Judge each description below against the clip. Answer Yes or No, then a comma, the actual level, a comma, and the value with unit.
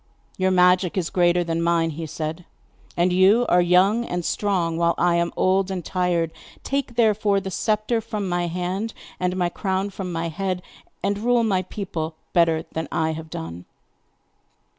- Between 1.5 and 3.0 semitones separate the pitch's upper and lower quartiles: Yes, average, 2.7 semitones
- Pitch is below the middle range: No, medium, 180 Hz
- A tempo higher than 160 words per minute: Yes, average, 170 wpm